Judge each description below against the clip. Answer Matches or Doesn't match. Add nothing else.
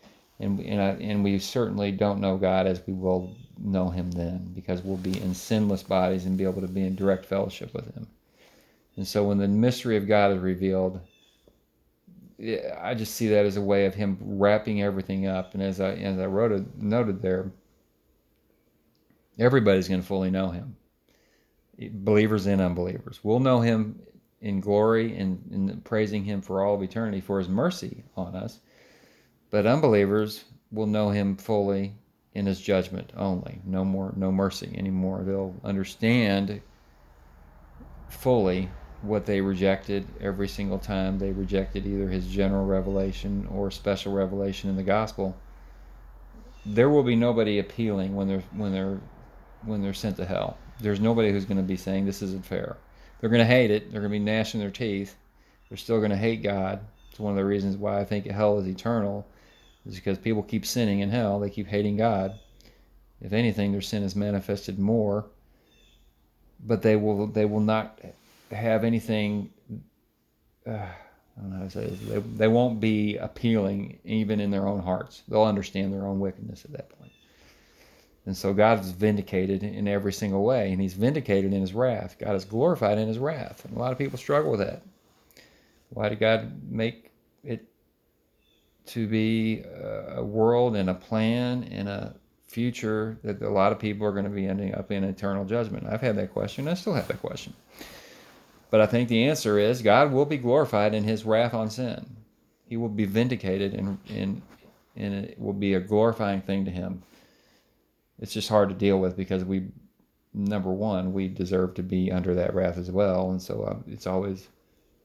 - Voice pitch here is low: Matches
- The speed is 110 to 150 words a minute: Doesn't match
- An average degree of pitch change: Doesn't match